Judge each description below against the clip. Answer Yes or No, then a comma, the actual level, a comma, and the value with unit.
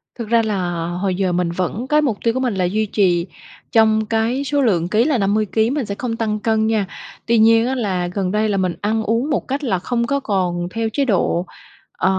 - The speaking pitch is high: Yes, high, 215 Hz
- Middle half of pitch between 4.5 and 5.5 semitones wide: No, average, 3.9 semitones